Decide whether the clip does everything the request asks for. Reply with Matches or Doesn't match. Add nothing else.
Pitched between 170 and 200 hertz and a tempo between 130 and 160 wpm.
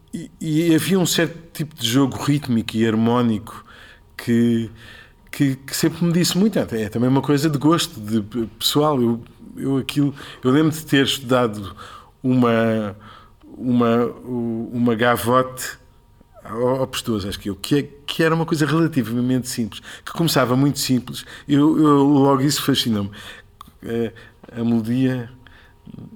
Doesn't match